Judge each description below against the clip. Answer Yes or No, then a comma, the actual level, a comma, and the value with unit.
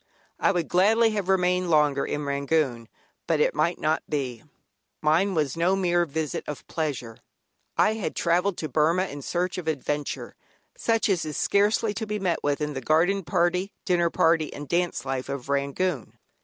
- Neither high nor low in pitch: Yes, medium, 165 Hz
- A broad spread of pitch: No, average, 4.1 semitones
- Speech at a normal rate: Yes, average, 175 wpm